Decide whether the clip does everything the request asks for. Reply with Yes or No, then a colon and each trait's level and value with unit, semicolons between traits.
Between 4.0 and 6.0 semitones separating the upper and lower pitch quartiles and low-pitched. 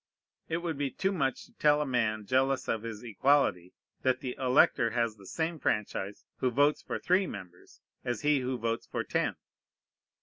Yes: average, 4.6 semitones; low, 130 Hz